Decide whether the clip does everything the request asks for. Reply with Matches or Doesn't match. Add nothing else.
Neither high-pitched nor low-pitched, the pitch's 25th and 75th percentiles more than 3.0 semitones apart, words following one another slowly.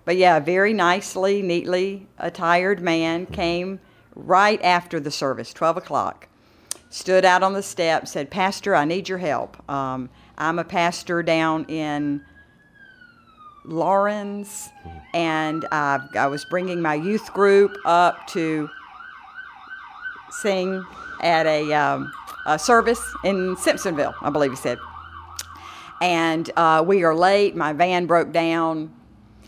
Matches